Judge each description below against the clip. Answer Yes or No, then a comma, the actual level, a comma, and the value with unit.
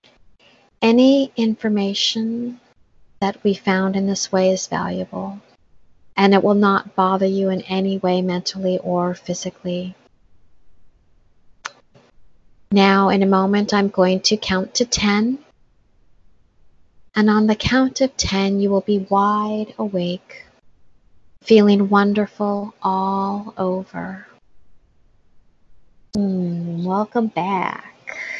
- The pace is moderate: No, slow, 105 wpm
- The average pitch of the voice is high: Yes, high, 195 Hz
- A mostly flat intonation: Yes, narrow, 2.1 semitones